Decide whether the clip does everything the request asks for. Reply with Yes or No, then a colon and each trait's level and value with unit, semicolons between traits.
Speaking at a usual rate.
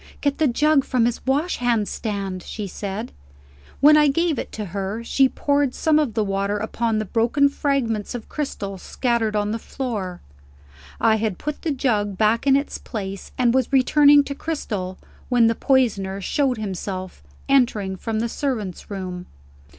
Yes: average, 165 wpm